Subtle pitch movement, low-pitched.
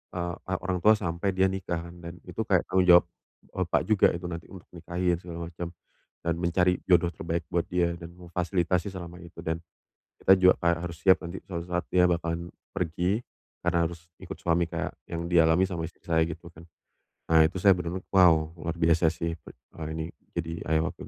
Yes: narrow, 1.5 semitones; very low, 85 Hz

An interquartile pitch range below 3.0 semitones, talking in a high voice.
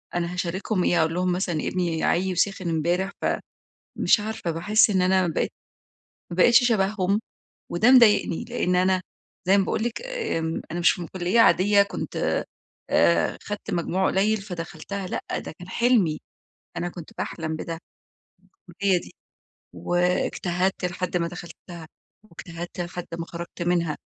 No: narrow, 2.6 semitones; medium, 180 Hz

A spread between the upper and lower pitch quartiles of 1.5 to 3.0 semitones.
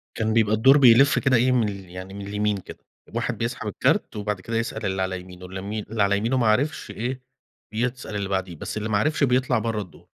No: average, 3.6 semitones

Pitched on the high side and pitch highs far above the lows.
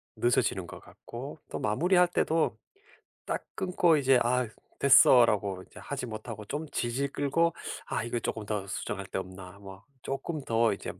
No: low, 120 Hz; wide, 5.7 semitones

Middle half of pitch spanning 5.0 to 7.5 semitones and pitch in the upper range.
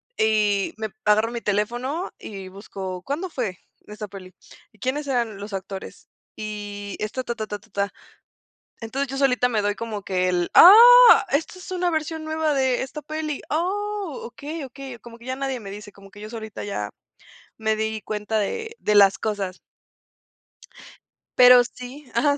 Yes: wide, 5.5 semitones; high, 230 Hz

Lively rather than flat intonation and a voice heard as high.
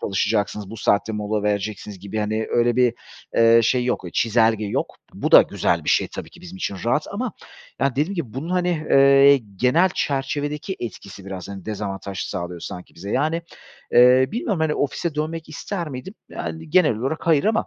No: wide, 6.8 semitones; low, 125 Hz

